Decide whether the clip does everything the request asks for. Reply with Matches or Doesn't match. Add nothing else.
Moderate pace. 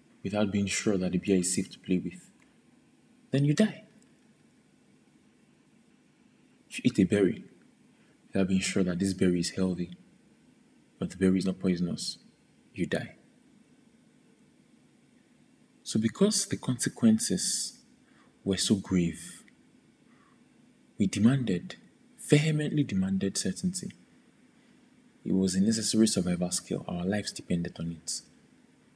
Doesn't match